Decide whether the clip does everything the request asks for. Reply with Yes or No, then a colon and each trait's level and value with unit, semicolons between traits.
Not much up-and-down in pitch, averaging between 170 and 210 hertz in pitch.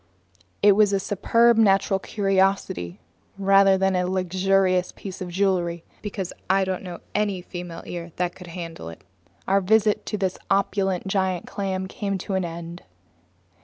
Yes: narrow, 1.7 semitones; high, 190 Hz